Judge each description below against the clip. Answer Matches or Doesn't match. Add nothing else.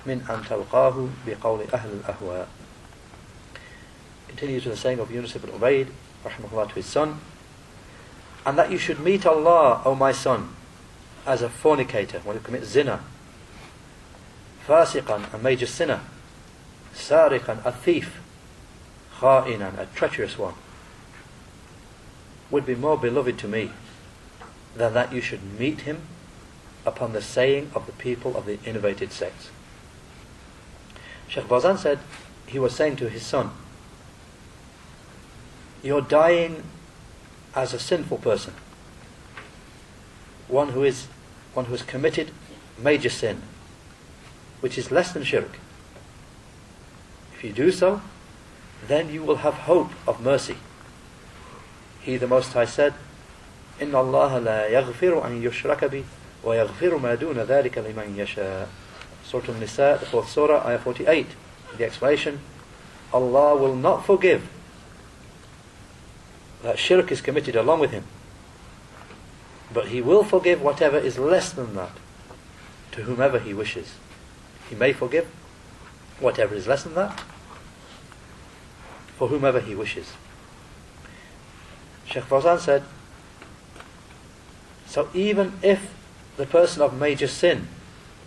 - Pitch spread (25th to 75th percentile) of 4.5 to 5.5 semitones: Matches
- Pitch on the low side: Matches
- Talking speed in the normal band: Doesn't match